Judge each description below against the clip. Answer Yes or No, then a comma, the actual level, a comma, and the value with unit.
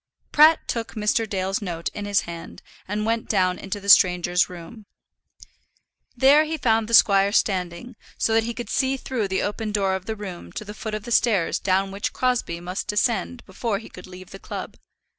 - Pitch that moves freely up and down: No, average, 3.4 semitones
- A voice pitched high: Yes, high, 205 Hz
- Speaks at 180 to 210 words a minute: Yes, average, 200 wpm